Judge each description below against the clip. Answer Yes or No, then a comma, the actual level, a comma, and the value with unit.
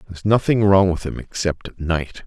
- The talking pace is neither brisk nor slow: No, fast, 210 wpm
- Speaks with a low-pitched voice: Yes, very low, 90 Hz